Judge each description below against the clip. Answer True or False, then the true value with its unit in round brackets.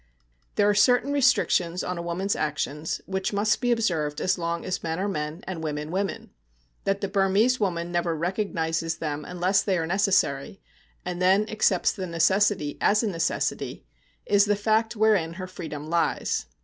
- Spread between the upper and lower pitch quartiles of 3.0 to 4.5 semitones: True (3.7 semitones)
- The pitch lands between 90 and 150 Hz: False (185 Hz)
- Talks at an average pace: True (170 wpm)